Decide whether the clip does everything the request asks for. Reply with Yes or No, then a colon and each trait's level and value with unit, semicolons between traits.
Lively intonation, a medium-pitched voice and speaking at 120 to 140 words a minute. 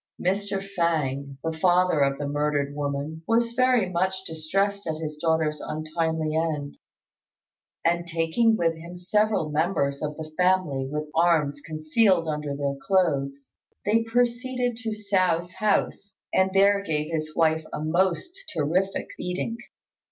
No: average, 4.3 semitones; medium, 165 Hz; slow, 135 wpm